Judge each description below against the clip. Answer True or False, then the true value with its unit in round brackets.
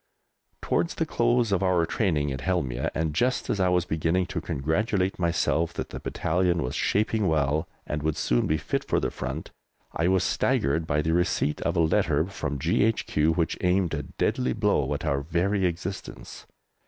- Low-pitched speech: True (85 Hz)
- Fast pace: False (180 wpm)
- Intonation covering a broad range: False (3.8 semitones)